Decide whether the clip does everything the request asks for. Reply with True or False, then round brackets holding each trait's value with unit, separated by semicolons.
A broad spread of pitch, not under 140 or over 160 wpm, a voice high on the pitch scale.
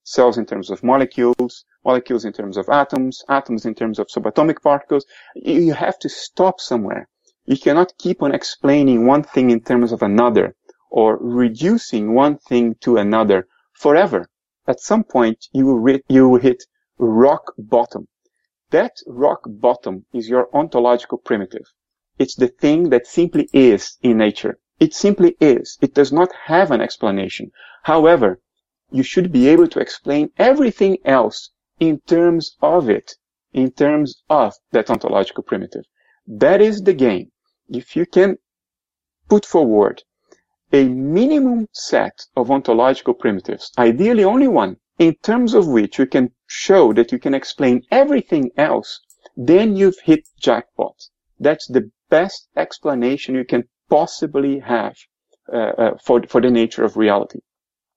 False (7.7 semitones; 150 wpm; 140 Hz)